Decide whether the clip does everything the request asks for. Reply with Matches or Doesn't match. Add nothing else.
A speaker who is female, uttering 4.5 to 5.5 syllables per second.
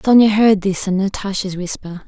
Matches